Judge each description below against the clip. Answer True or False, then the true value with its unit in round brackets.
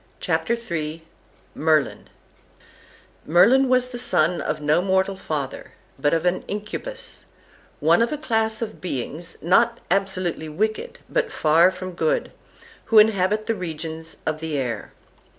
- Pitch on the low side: False (185 Hz)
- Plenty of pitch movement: True (5.8 semitones)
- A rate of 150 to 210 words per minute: False (135 wpm)